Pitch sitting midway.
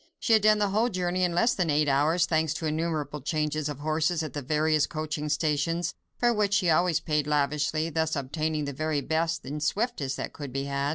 Yes: medium, 155 Hz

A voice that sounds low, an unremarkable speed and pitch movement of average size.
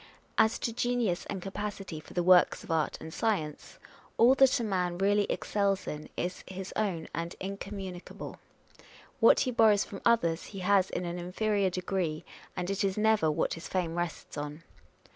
No: high, 190 Hz; average, 180 wpm; average, 3.1 semitones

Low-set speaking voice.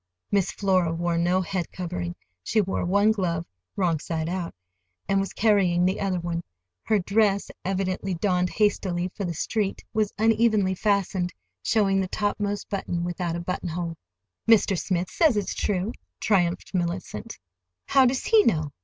No: high, 190 Hz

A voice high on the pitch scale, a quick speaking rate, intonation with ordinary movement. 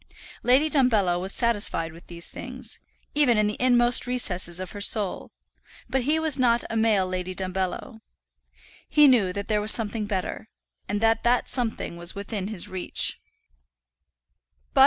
No: high, 215 Hz; average, 155 wpm; average, 4.7 semitones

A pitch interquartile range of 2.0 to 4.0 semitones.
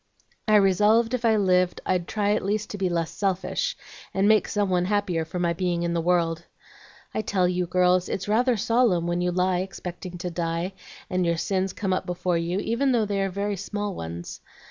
Yes: average, 2.7 semitones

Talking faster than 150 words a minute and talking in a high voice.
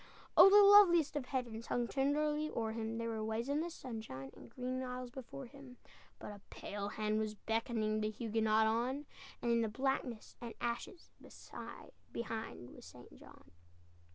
Yes: average, 160 wpm; high, 235 Hz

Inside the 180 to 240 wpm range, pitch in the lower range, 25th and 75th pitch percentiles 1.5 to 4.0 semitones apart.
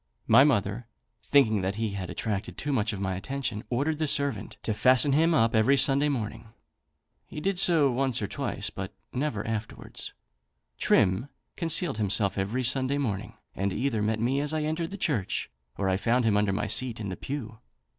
No: average, 185 wpm; low, 120 Hz; average, 5.3 semitones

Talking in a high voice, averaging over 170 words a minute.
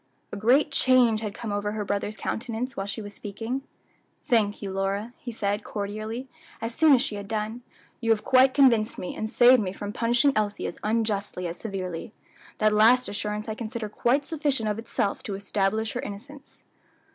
Yes: high, 220 Hz; average, 185 wpm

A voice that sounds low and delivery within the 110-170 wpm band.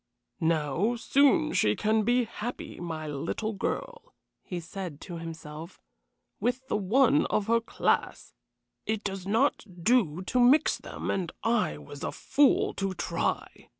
No: high, 205 Hz; average, 145 wpm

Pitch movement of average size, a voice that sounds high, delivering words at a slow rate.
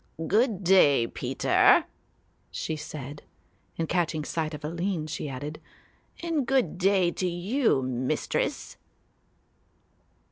No: average, 4.6 semitones; medium, 170 Hz; slow, 105 wpm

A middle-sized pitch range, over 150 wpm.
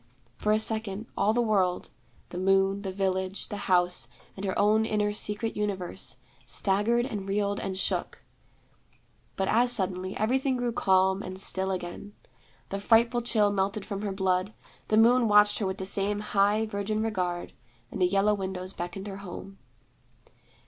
No: narrow, 2.1 semitones; average, 160 wpm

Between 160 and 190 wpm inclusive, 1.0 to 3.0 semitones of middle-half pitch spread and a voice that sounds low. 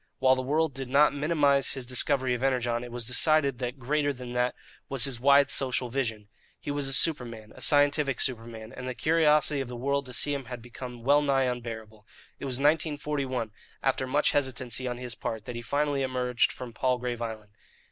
No: average, 200 wpm; narrow, 2.6 semitones; low, 130 Hz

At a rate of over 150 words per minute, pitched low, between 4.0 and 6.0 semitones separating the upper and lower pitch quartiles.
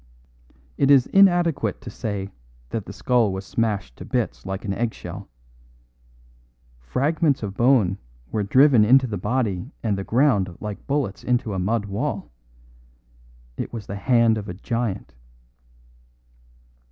No: average, 140 wpm; low, 110 Hz; average, 4.8 semitones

